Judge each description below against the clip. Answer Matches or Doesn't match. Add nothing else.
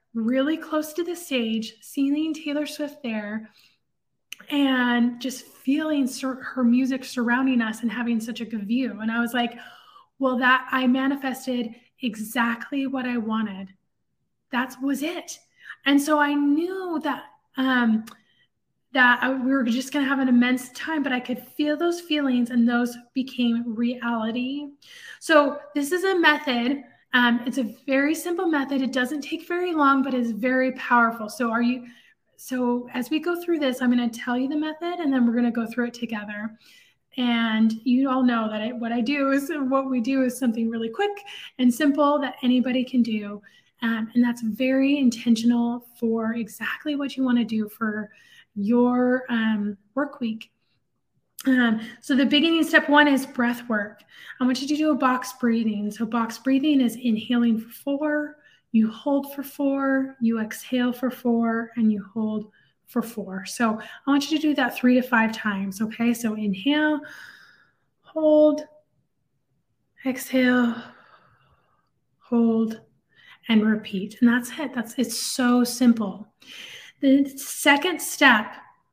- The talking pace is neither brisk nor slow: Matches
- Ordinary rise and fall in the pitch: Matches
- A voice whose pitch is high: Matches